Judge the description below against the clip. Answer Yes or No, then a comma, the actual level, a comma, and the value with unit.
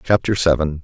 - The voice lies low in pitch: Yes, very low, 85 Hz